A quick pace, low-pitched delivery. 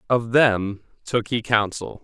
No: average, 145 wpm; low, 110 Hz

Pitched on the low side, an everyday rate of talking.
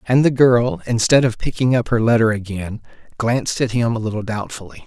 Yes: low, 115 Hz; average, 195 wpm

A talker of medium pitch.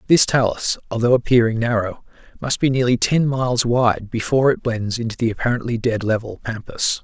No: low, 120 Hz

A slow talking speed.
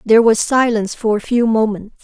No: fast, 205 wpm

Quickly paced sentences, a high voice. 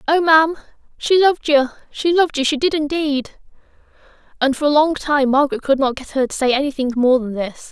Yes: fast, 210 wpm; very high, 290 Hz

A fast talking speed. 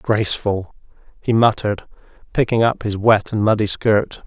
No: average, 140 wpm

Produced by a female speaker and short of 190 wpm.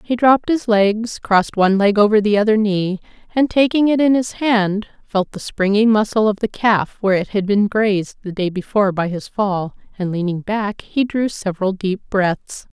No: female; average, 200 wpm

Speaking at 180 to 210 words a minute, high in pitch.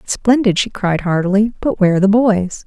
Yes: fast, 205 wpm; high, 200 Hz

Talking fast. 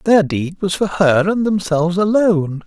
No: average, 180 wpm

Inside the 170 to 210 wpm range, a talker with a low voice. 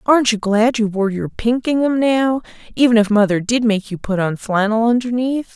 No: fast, 205 wpm; high, 225 Hz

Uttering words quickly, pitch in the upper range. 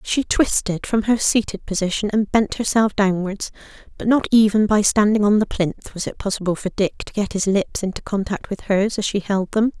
Yes: fast, 215 wpm; high, 205 Hz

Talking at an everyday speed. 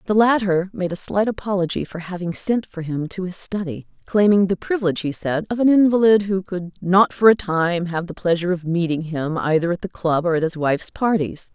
No: fast, 220 wpm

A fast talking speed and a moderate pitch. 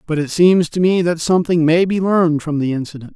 Yes: fast, 245 wpm; medium, 165 Hz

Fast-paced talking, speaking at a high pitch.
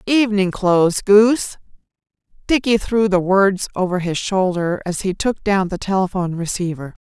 No: average, 145 wpm; high, 195 Hz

